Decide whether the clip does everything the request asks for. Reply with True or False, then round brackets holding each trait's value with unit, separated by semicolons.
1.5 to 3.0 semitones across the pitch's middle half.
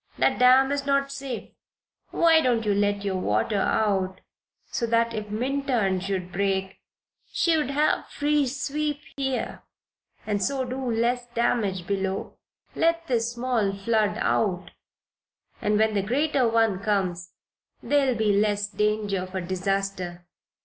False (5.1 semitones)